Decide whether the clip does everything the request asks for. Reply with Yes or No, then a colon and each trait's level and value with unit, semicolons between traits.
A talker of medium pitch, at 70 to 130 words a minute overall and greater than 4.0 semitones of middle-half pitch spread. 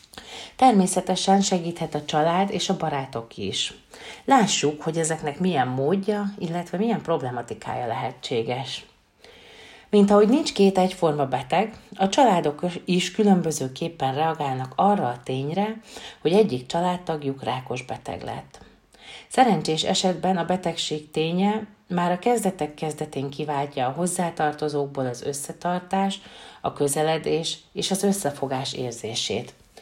Yes: medium, 170 Hz; average, 115 wpm; average, 5.2 semitones